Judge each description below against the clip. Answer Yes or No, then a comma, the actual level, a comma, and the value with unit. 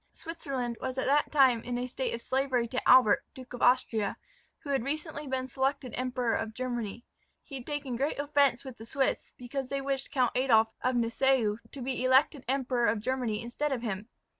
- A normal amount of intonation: No, narrow, 2.3 semitones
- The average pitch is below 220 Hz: No, very high, 255 Hz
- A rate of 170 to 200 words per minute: Yes, average, 195 wpm